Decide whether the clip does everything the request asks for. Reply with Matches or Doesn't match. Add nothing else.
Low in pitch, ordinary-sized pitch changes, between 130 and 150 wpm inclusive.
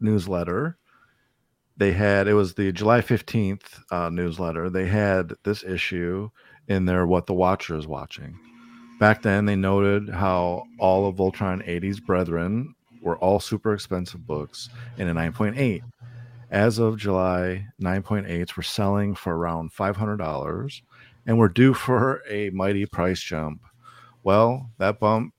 Matches